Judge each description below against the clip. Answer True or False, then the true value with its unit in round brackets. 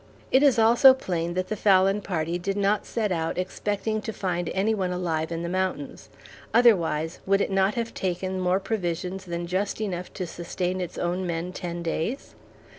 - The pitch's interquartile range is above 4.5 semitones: False (2.9 semitones)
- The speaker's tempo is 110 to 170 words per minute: False (185 wpm)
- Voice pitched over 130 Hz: True (185 Hz)